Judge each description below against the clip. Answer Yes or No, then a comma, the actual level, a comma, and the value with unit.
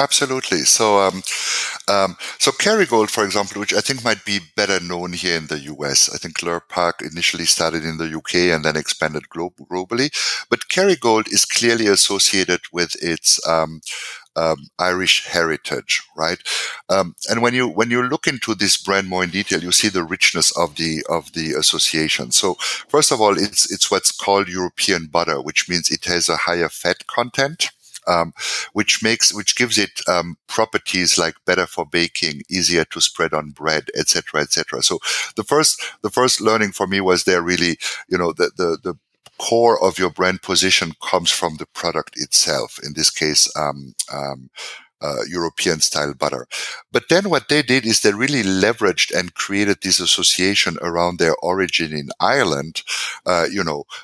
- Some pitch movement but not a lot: Yes, average, 4.1 semitones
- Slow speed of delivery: No, average, 180 wpm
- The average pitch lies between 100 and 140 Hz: No, very low, 90 Hz